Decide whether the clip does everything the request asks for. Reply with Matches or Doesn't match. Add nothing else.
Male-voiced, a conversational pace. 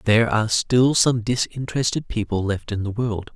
Matches